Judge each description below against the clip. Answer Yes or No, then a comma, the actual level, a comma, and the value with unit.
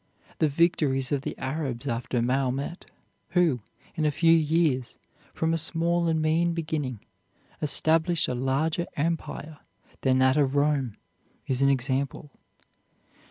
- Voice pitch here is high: No, medium, 150 Hz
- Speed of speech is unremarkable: No, slow, 130 wpm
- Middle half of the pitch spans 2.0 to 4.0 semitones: Yes, average, 3.6 semitones